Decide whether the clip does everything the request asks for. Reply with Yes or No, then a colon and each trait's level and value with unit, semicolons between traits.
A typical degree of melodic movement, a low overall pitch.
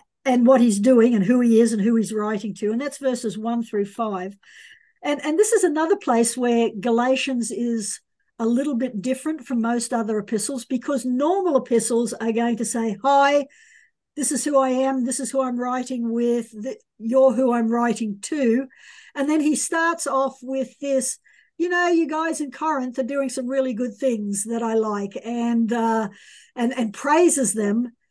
No: average, 3.0 semitones; very high, 250 Hz